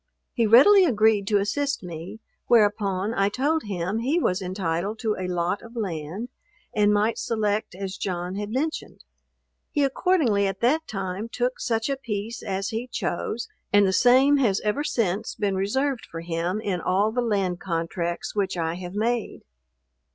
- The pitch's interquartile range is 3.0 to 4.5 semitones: Yes, average, 4.0 semitones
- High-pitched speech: Yes, high, 205 Hz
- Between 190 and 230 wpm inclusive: No, average, 165 wpm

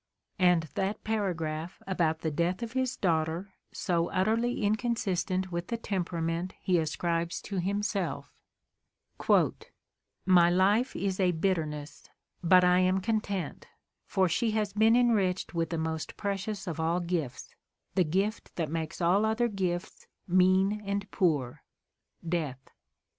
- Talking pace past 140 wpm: No, slow, 135 wpm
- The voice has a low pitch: No, medium, 185 Hz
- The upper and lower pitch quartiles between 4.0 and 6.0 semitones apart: No, average, 3.3 semitones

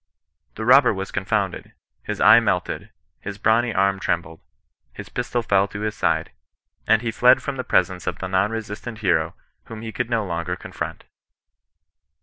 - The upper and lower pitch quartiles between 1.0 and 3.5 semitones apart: Yes, average, 3.2 semitones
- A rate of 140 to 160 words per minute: No, average, 170 wpm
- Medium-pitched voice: No, low, 105 Hz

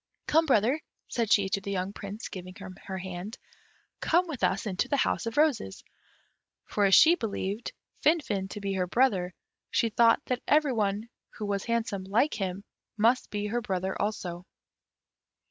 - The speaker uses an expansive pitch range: No, average, 3.9 semitones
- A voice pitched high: Yes, high, 205 Hz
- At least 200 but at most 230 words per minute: No, average, 170 wpm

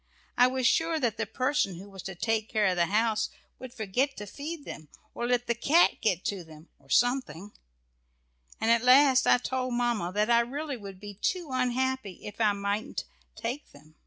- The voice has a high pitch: Yes, high, 230 Hz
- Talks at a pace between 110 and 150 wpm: No, average, 195 wpm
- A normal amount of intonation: Yes, average, 4.3 semitones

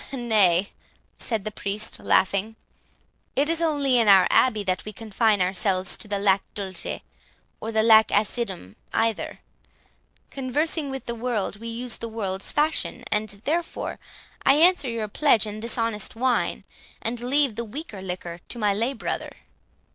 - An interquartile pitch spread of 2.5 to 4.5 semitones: Yes, average, 3.8 semitones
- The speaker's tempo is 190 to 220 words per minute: No, average, 155 wpm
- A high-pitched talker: Yes, high, 225 Hz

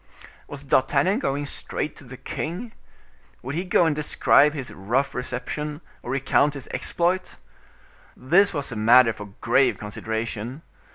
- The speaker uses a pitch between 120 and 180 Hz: Yes, medium, 140 Hz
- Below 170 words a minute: Yes, average, 145 wpm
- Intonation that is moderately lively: Yes, average, 3.6 semitones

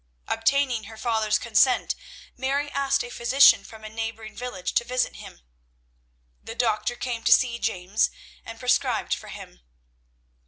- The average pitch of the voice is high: Yes, high, 235 Hz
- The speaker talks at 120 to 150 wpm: Yes, average, 145 wpm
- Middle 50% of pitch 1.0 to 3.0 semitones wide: Yes, narrow, 2.5 semitones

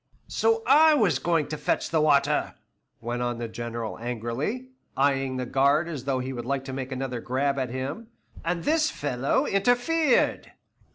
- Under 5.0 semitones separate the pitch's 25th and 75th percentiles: No, wide, 5.4 semitones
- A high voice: No, medium, 140 Hz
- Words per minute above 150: Yes, average, 170 wpm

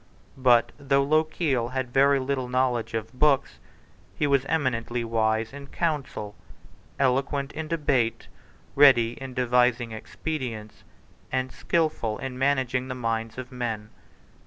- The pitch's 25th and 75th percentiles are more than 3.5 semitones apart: No, average, 3.0 semitones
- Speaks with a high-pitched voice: No, low, 130 Hz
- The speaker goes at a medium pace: No, slow, 125 wpm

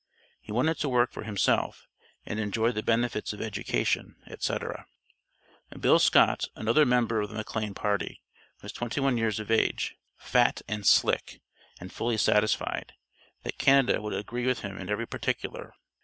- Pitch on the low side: Yes, low, 110 Hz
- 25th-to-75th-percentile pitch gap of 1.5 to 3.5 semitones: Yes, narrow, 2.4 semitones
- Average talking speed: Yes, average, 155 wpm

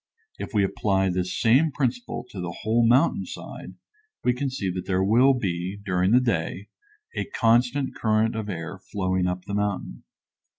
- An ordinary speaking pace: Yes, average, 170 wpm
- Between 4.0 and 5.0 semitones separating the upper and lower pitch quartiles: Yes, average, 4.7 semitones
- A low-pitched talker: Yes, low, 105 Hz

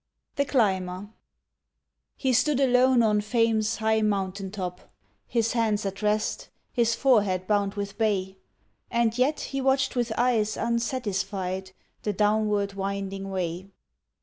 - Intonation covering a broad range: No, average, 3.3 semitones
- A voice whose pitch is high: Yes, high, 210 Hz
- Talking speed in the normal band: No, slow, 125 wpm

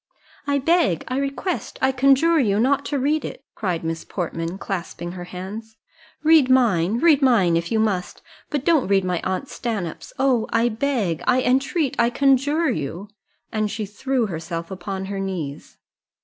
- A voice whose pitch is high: Yes, high, 225 Hz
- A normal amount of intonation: No, wide, 6.8 semitones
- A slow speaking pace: No, average, 165 wpm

